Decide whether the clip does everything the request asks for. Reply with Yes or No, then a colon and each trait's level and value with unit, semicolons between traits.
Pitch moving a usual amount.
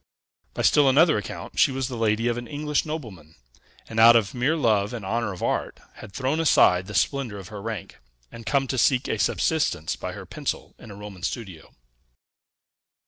Yes: average, 4.9 semitones